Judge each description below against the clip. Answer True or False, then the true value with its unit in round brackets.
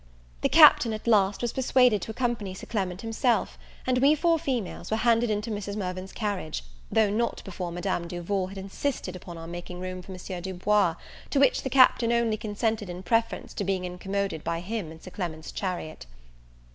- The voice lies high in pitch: True (200 Hz)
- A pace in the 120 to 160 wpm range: False (190 wpm)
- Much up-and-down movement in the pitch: False (4.0 semitones)